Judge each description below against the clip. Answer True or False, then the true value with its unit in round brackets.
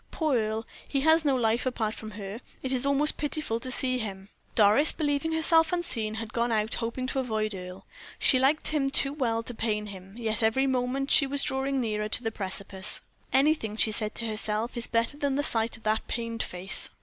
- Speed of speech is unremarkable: False (210 wpm)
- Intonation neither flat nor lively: True (4.0 semitones)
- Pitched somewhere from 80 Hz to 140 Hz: False (235 Hz)